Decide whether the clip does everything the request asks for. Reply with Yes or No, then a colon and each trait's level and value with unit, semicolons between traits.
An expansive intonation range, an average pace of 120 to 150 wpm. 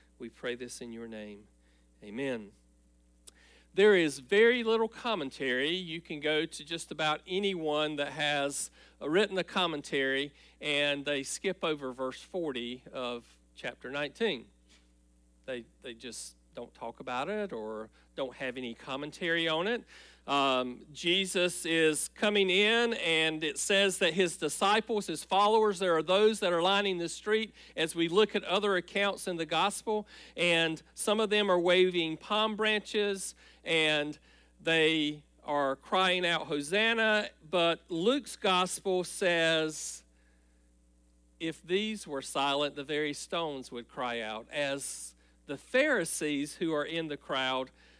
Yes: wide, 6.4 semitones; average, 140 wpm